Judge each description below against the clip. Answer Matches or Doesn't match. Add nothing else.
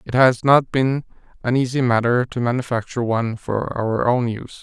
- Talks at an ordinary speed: Matches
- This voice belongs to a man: Matches